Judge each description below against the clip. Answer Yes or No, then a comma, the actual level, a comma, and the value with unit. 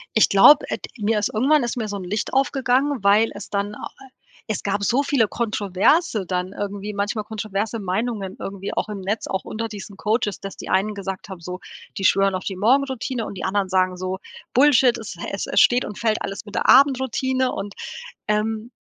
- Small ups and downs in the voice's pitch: No, average, 3.5 semitones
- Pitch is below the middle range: No, high, 210 Hz